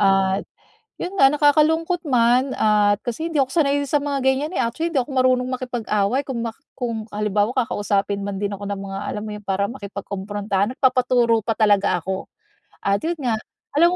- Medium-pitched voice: No, high, 235 Hz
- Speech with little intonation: No, average, 4.9 semitones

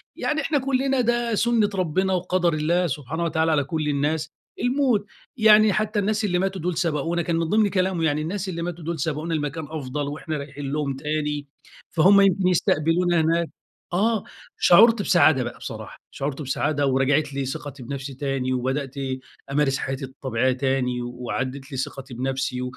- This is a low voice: No, medium, 155 Hz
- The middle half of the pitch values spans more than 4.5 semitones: Yes, average, 5.2 semitones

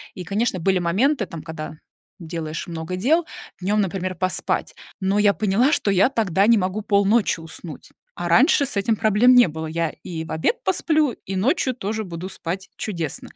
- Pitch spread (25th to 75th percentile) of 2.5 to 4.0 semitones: No, average, 4.9 semitones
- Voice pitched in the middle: No, high, 195 Hz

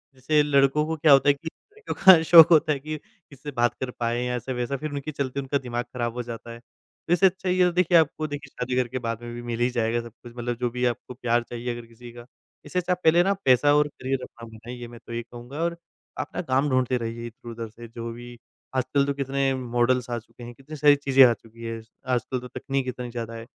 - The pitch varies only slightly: No, average, 3.4 semitones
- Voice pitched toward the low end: Yes, low, 125 Hz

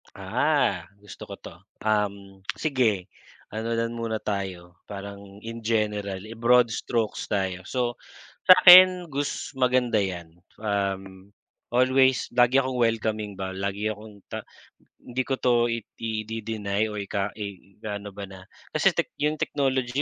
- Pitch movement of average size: Yes, average, 3.6 semitones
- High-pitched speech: No, low, 110 Hz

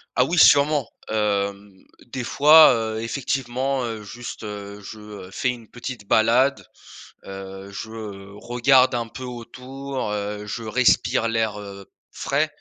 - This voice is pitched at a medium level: No, low, 115 Hz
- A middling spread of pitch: Yes, average, 3.6 semitones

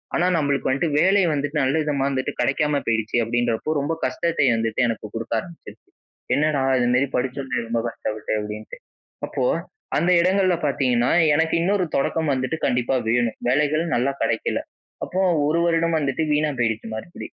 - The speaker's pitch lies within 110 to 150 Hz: Yes, medium, 140 Hz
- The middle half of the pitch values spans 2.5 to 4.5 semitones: No, average, 5.0 semitones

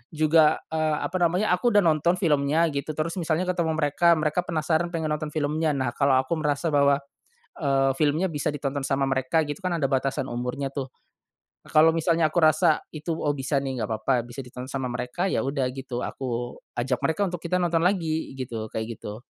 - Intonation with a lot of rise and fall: No, average, 3.4 semitones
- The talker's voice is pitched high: No, medium, 150 Hz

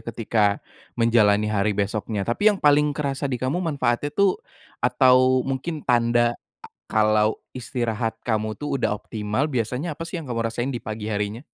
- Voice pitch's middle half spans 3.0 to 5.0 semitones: Yes, average, 4.2 semitones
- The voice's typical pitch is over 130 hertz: No, low, 120 Hz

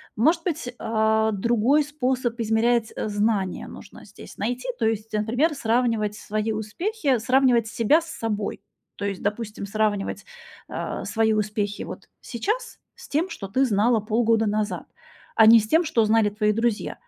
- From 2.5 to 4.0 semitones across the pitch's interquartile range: Yes, average, 2.8 semitones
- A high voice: Yes, high, 225 Hz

